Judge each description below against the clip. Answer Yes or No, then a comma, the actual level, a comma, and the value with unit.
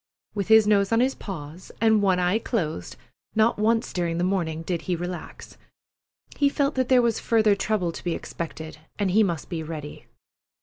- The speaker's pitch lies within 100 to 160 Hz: No, high, 195 Hz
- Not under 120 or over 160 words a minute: No, average, 185 wpm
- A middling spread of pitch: Yes, average, 4.6 semitones